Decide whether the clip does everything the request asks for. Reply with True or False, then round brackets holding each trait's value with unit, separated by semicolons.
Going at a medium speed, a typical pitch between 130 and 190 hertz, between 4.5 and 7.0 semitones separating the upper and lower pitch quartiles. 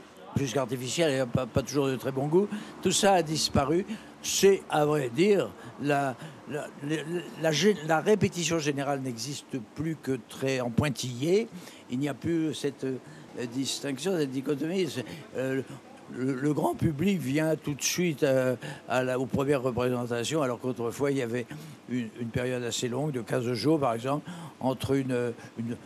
False (170 wpm; 140 Hz; 3.9 semitones)